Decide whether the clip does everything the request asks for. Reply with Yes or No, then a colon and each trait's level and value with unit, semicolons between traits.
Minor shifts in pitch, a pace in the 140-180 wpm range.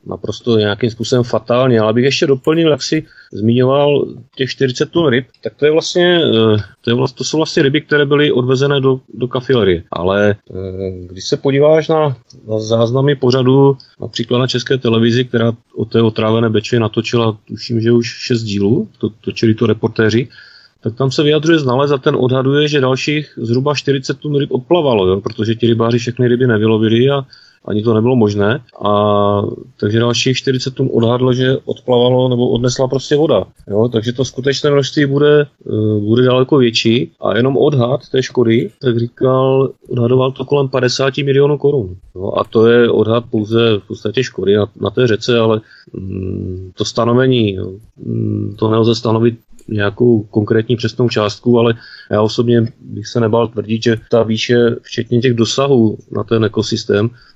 No: average, 3.1 semitones; fast, 170 wpm